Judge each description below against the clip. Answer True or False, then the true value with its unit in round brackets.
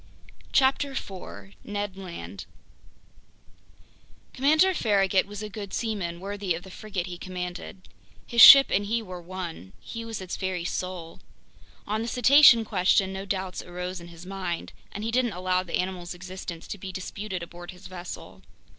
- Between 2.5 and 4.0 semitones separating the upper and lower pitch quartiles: True (2.8 semitones)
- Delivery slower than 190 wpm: True (160 wpm)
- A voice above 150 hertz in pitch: True (190 Hz)